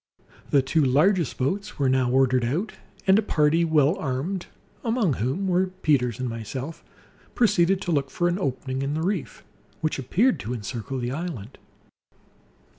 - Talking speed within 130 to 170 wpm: Yes, average, 160 wpm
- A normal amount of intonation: No, wide, 5.9 semitones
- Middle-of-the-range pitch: Yes, medium, 150 Hz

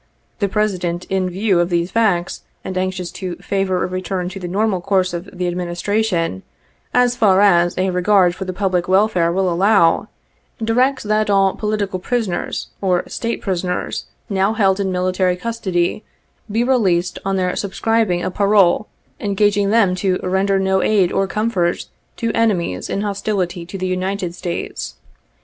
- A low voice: No, high, 190 Hz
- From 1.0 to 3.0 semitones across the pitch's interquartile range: Yes, narrow, 2.4 semitones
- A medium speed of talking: Yes, average, 165 wpm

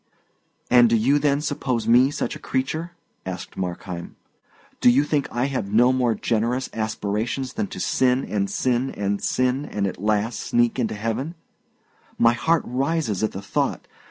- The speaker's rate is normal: Yes, average, 165 wpm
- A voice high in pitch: No, low, 120 Hz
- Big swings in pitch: No, average, 3.8 semitones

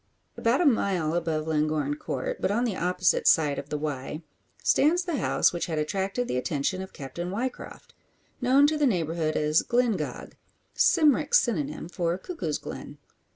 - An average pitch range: No, wide, 8.2 semitones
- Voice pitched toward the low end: No, medium, 180 Hz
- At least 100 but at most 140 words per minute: No, average, 160 wpm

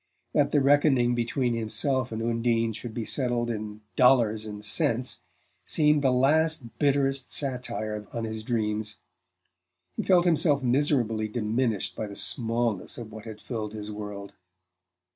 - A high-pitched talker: No, low, 120 Hz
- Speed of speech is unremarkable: Yes, average, 145 wpm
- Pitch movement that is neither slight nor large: Yes, average, 3.6 semitones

